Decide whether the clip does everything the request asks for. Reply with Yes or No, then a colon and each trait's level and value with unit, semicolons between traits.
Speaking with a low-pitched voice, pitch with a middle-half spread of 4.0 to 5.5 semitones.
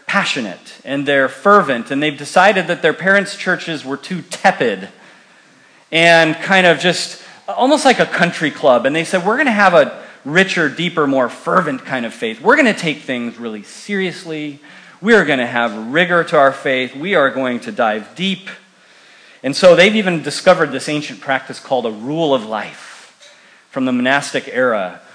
No: medium, 160 Hz; average, 5.1 semitones